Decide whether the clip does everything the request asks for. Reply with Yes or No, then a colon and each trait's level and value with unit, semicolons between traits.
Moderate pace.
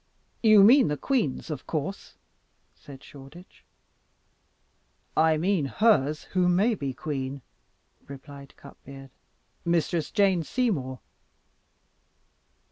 No: slow, 95 wpm